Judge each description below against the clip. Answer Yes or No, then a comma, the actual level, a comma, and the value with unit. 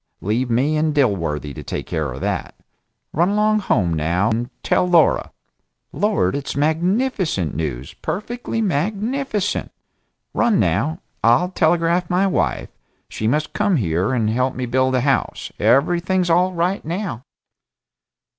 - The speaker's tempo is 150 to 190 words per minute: No, slow, 135 wpm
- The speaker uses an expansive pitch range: Yes, wide, 8.8 semitones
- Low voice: No, medium, 155 Hz